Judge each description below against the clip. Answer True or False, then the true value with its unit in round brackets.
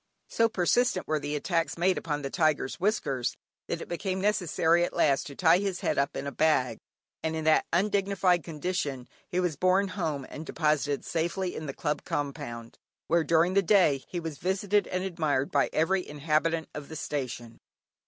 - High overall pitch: False (160 Hz)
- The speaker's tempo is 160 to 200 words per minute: True (185 wpm)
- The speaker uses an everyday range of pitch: True (4.0 semitones)